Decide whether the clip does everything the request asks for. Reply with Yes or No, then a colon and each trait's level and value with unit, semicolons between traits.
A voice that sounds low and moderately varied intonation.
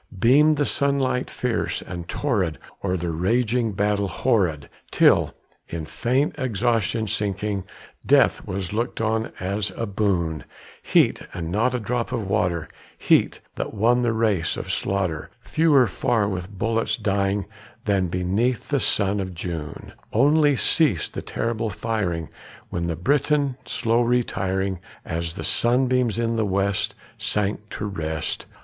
Yes: low, 105 Hz; average, 4.5 semitones